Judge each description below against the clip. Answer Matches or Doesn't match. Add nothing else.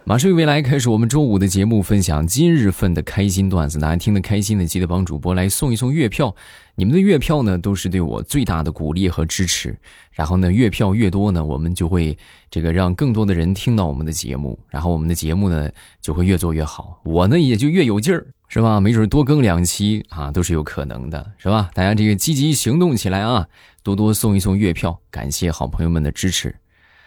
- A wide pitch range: Doesn't match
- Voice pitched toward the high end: Doesn't match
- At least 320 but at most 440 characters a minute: Matches